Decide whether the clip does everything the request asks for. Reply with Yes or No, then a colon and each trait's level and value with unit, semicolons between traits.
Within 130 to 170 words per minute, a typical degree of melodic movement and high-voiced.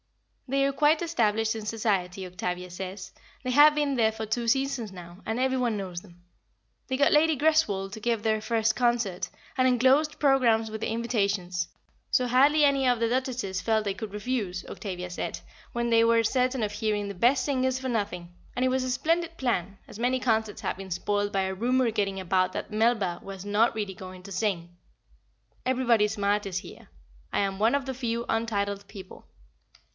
No: average, 190 wpm; average, 4.4 semitones; high, 220 Hz